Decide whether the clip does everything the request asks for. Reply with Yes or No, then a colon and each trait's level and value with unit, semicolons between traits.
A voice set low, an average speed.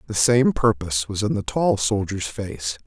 Yes: low, 100 Hz; average, 190 wpm